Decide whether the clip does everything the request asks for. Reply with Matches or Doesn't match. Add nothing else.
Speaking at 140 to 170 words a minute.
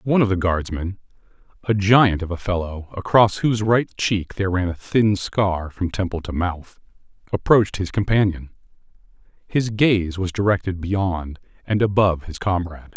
Matches